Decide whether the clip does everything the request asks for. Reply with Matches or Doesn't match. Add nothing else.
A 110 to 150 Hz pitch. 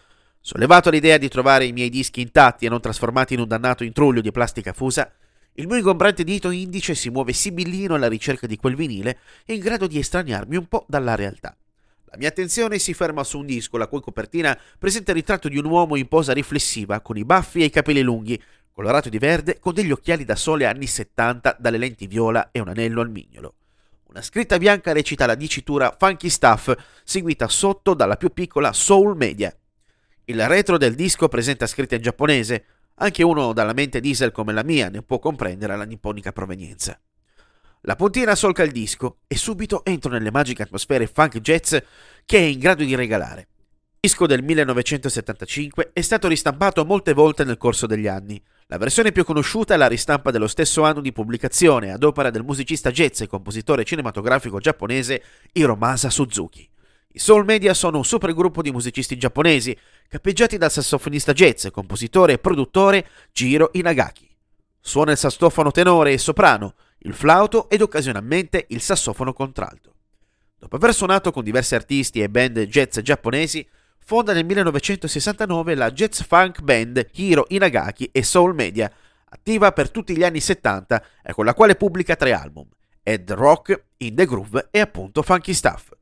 Matches